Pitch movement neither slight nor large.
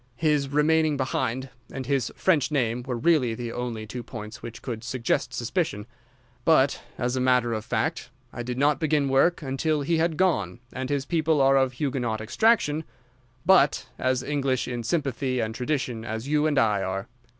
Yes: average, 3.9 semitones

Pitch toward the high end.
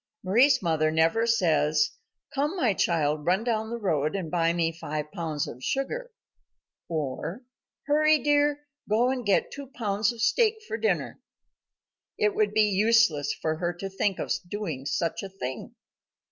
Yes: high, 195 Hz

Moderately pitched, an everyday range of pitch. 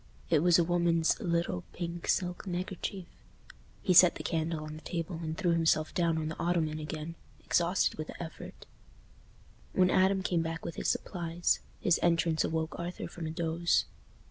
No: medium, 170 Hz; narrow, 1.6 semitones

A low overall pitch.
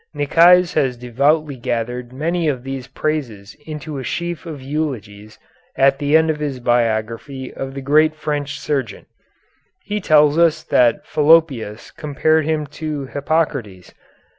No: medium, 145 Hz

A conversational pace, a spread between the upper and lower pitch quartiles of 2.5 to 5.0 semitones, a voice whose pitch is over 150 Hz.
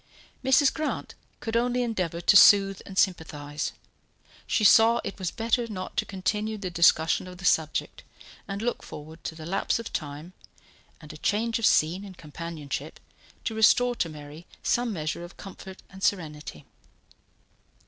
No: average, 160 wpm; wide, 5.5 semitones; medium, 185 Hz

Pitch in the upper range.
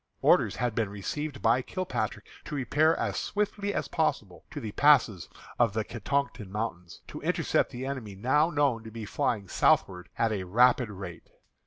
No: low, 115 Hz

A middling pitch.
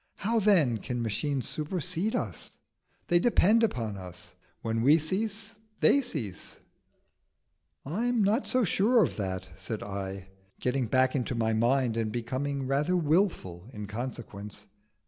No: low, 130 Hz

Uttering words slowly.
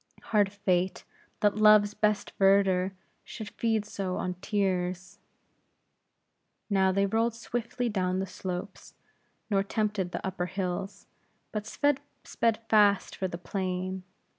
Yes: slow, 120 wpm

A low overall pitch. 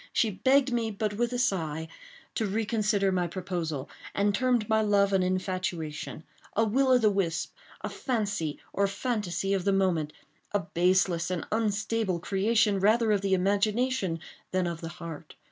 No: high, 200 Hz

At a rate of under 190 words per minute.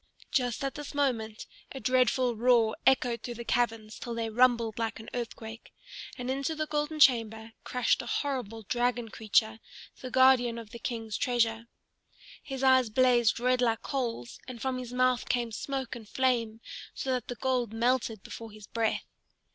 Yes: average, 170 wpm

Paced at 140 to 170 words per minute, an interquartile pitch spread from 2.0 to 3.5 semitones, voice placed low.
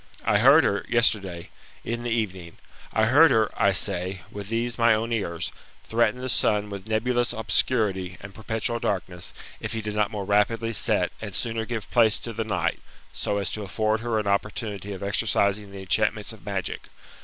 No: average, 185 wpm; narrow, 2.4 semitones; low, 105 Hz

